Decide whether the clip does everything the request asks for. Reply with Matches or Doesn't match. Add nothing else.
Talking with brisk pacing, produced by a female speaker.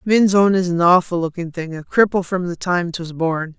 Matches